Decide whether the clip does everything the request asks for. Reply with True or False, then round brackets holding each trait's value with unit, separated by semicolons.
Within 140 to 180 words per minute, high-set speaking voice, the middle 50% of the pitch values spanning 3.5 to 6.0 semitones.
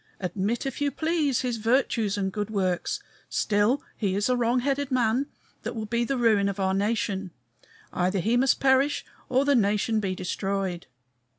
True (175 wpm; 220 Hz; 4.5 semitones)